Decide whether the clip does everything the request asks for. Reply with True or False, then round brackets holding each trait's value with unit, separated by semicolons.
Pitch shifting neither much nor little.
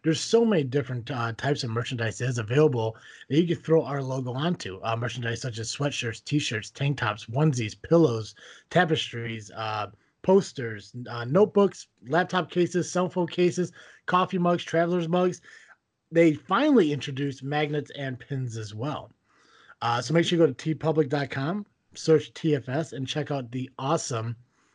False (5.7 semitones)